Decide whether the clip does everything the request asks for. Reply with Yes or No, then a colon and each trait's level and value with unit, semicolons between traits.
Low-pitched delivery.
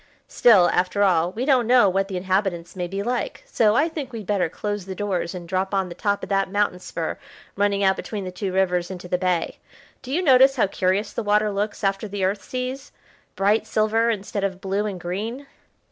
No: high, 200 Hz